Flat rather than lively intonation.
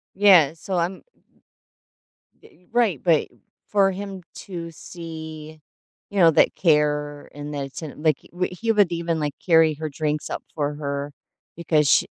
No: average, 3.4 semitones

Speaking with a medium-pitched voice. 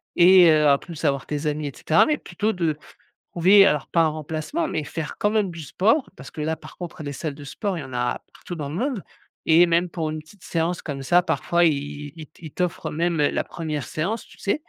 Yes: medium, 165 Hz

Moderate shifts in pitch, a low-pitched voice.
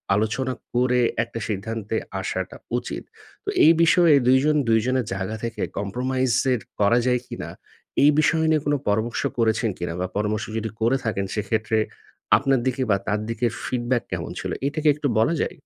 Yes: average, 3.4 semitones; low, 115 Hz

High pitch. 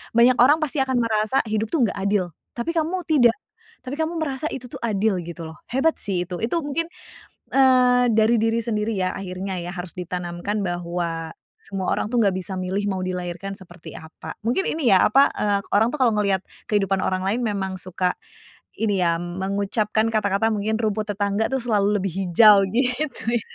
Yes: high, 210 Hz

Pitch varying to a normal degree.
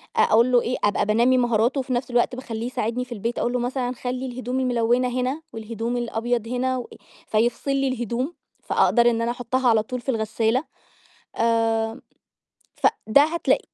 No: narrow, 1.9 semitones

